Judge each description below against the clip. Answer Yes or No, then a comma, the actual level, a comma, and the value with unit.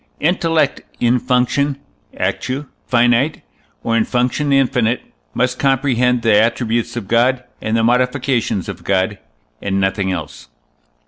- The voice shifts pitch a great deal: No, average, 2.8 semitones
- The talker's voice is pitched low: Yes, low, 120 Hz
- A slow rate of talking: Yes, slow, 125 wpm